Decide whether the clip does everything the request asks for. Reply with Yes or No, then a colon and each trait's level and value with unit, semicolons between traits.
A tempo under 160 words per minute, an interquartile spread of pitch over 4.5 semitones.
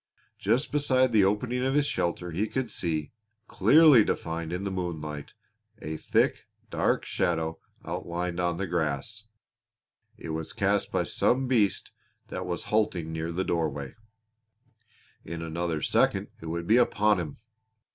Yes: average, 145 wpm; average, 5.0 semitones